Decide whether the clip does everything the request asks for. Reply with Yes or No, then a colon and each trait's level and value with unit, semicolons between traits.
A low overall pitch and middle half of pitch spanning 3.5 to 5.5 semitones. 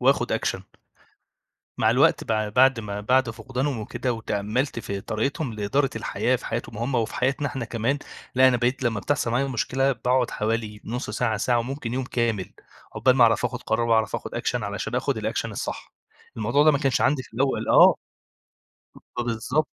No: low, 120 Hz; average, 2.9 semitones